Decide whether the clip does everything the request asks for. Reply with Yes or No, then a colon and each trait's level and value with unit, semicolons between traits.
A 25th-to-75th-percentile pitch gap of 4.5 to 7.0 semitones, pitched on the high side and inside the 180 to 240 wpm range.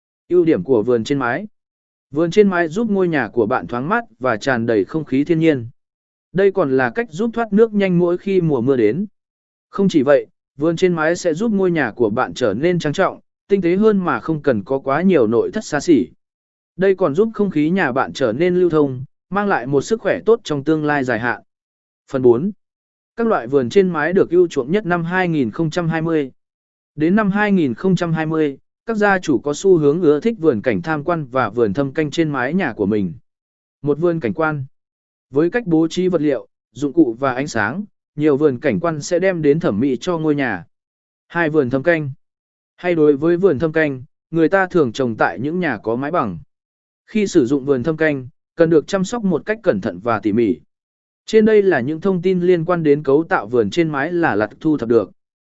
No: average, 5.2 semitones; medium, 165 Hz; average, 225 wpm